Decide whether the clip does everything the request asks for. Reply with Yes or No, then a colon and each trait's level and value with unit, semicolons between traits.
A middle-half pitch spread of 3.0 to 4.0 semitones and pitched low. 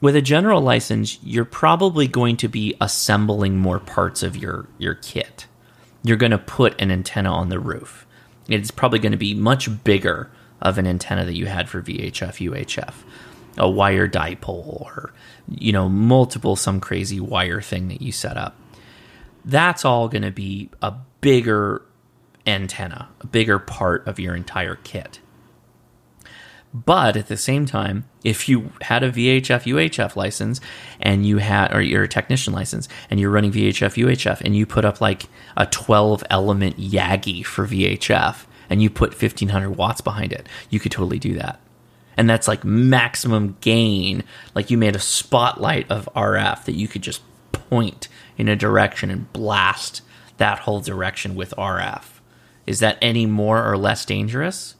Yes: average, 3.3 semitones; low, 105 Hz